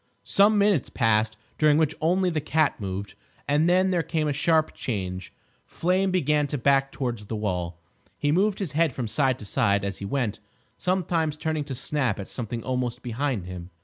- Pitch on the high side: No, medium, 140 Hz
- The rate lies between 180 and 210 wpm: Yes, average, 185 wpm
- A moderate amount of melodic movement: No, wide, 6.6 semitones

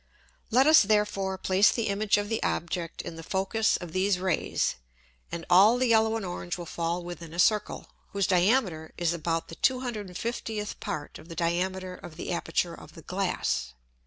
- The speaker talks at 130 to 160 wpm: No, average, 180 wpm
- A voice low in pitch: No, medium, 185 Hz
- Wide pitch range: No, average, 3.7 semitones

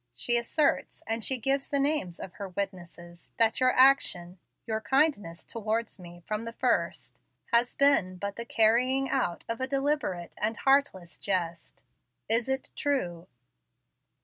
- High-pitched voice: Yes, high, 225 Hz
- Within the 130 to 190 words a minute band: Yes, average, 150 wpm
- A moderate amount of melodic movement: No, wide, 6.5 semitones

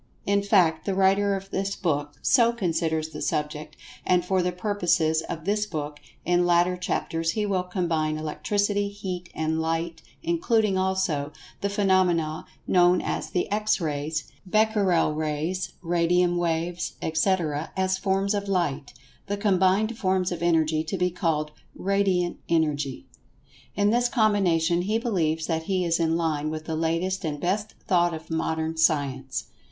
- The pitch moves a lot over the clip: No, average, 3.5 semitones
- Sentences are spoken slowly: No, average, 150 wpm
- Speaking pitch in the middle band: Yes, medium, 175 Hz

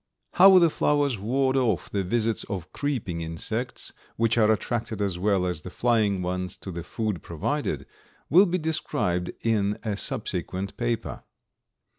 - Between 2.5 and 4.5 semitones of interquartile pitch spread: No, average, 5.3 semitones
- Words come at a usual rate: Yes, average, 150 wpm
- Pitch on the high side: No, low, 110 Hz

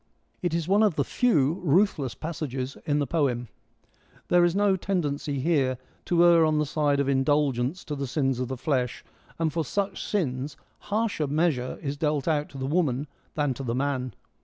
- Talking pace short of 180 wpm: No, average, 185 wpm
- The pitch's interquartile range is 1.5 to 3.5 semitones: No, average, 4.0 semitones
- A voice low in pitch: No, medium, 150 Hz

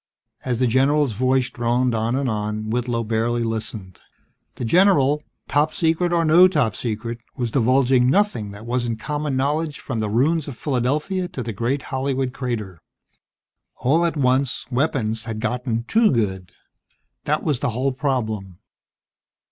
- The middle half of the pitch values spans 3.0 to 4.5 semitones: Yes, average, 4.1 semitones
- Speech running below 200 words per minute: Yes, average, 150 wpm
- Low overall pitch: Yes, low, 125 Hz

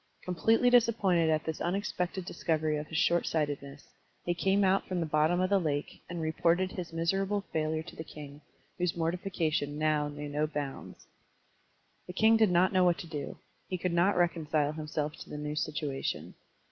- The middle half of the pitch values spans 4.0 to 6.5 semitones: No, average, 3.2 semitones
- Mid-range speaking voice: Yes, medium, 165 Hz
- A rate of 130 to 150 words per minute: No, average, 175 wpm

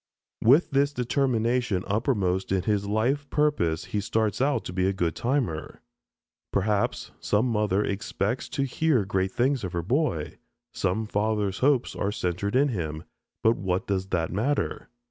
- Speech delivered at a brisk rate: No, average, 155 wpm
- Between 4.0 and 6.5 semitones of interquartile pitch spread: Yes, average, 5.2 semitones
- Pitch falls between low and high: No, low, 105 Hz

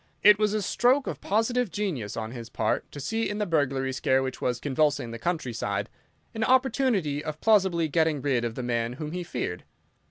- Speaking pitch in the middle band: Yes, medium, 150 Hz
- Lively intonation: Yes, wide, 8.8 semitones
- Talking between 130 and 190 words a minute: No, average, 200 wpm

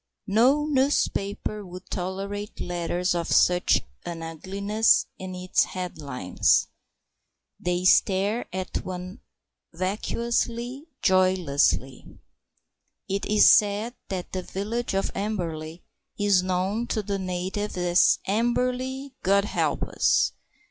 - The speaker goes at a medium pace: No, slow, 105 wpm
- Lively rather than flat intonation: No, average, 2.9 semitones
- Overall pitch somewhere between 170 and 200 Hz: Yes, high, 190 Hz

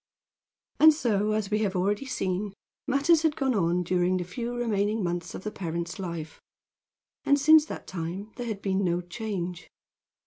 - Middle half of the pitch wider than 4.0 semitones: Yes, average, 5.0 semitones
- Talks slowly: No, average, 170 wpm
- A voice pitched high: Yes, high, 200 Hz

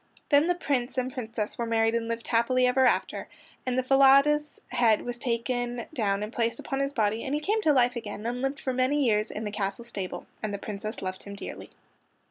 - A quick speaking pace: Yes, fast, 215 wpm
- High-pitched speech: Yes, high, 240 Hz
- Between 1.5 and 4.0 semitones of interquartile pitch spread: Yes, average, 3.4 semitones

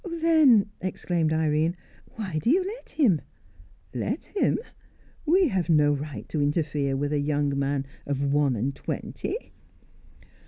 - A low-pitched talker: No, medium, 155 Hz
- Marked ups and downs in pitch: Yes, wide, 6.8 semitones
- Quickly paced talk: No, average, 140 wpm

